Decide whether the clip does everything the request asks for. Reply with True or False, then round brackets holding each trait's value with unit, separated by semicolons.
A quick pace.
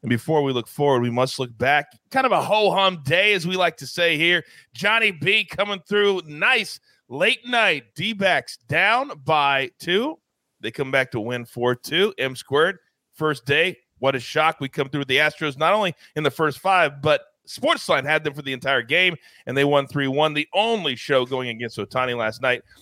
True (210 wpm)